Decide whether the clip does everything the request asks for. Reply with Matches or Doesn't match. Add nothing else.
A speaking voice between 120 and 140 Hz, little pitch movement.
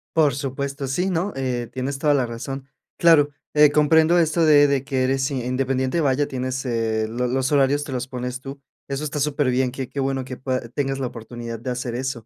Matches